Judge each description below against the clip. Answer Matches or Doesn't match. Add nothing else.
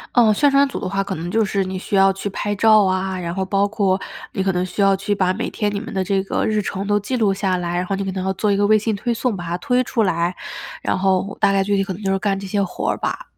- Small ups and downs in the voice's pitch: Matches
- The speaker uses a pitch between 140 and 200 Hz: Matches